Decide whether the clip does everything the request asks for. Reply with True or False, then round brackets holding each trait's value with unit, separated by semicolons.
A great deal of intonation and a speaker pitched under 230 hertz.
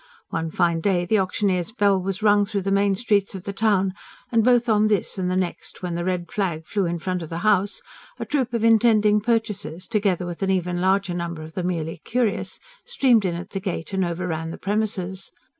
False (3.2 semitones; 190 Hz)